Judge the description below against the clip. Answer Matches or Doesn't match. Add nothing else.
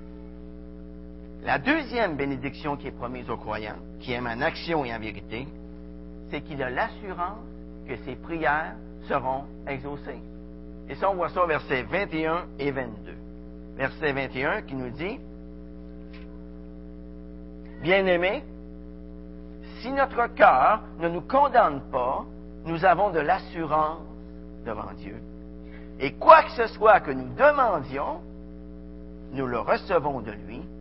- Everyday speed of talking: Doesn't match